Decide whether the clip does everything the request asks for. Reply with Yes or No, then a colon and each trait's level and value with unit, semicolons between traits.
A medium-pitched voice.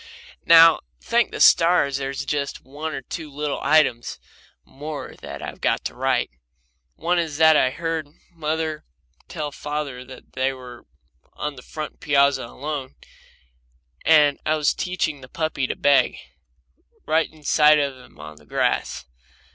Yes: medium, 150 Hz